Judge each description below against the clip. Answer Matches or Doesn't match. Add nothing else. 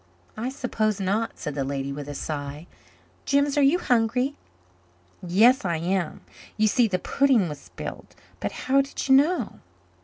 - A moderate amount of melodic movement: Doesn't match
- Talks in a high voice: Matches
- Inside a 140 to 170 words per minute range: Matches